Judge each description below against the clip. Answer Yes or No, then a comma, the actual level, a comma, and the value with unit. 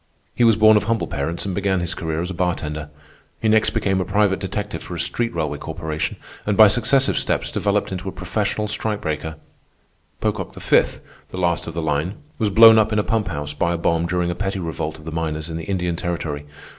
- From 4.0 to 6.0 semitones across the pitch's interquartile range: Yes, average, 4.4 semitones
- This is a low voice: Yes, very low, 90 Hz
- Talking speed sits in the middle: No, fast, 220 wpm